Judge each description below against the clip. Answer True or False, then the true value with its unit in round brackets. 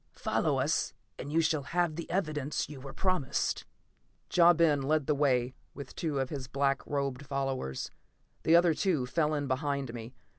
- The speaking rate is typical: True (175 wpm)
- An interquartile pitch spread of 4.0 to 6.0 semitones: False (2.9 semitones)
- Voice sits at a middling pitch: True (145 Hz)